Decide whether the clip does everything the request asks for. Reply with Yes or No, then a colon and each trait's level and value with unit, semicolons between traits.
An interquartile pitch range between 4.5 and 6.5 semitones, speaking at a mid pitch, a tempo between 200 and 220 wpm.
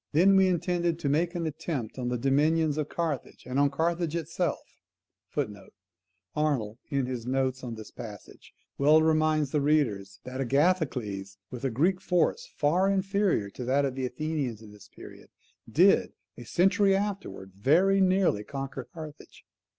No: average, 5.2 semitones; medium, 150 Hz; average, 155 wpm